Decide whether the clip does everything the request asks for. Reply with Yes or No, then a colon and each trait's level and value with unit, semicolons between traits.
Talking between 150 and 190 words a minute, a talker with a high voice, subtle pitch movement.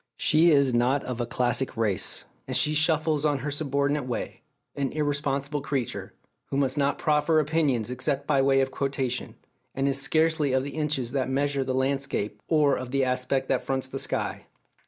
No: average, 180 wpm; medium, 140 Hz; narrow, 2.1 semitones